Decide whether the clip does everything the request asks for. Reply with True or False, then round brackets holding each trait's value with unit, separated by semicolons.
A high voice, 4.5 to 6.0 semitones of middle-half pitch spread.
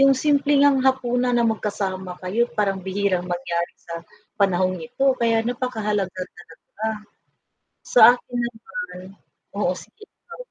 True (215 Hz; 5.1 semitones)